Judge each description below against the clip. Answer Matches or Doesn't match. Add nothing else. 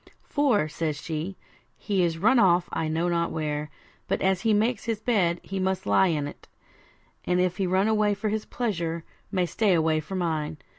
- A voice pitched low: Doesn't match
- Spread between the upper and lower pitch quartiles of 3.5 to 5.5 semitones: Matches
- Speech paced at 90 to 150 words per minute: Doesn't match